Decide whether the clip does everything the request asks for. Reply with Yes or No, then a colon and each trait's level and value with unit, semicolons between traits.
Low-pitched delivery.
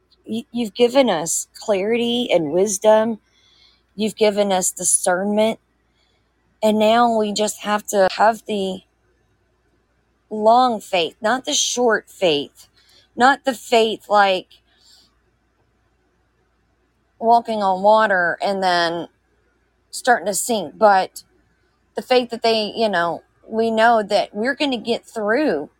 No: high, 215 Hz